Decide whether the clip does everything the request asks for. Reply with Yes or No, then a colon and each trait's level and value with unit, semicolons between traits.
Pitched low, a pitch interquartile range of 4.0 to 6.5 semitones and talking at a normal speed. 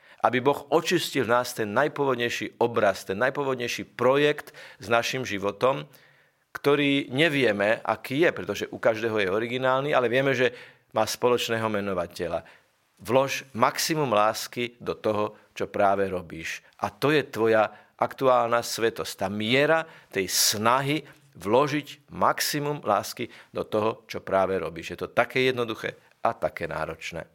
Yes: low, 120 Hz; average, 4.6 semitones; average, 135 wpm